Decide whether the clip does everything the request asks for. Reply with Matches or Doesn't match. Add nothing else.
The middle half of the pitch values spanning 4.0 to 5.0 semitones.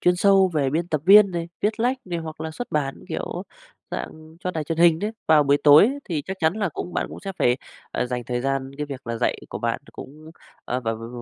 Matches